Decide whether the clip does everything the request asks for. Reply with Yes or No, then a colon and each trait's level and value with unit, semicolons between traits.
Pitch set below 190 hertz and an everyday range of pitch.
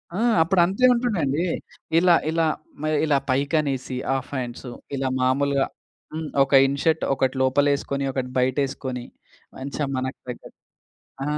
Yes: medium, 140 Hz; average, 3.2 semitones